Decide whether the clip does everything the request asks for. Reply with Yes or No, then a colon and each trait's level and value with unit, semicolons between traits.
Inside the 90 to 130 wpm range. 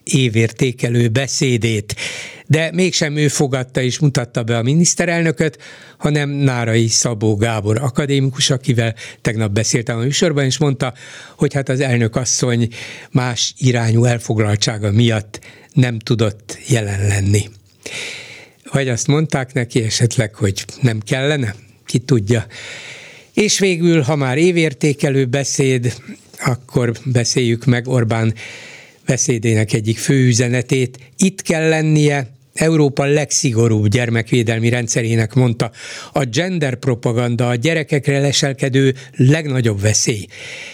Yes: average, 110 wpm